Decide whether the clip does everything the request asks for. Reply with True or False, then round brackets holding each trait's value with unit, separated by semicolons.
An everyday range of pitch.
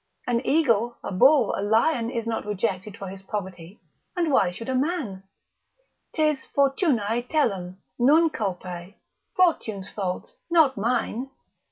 False (6.2 semitones)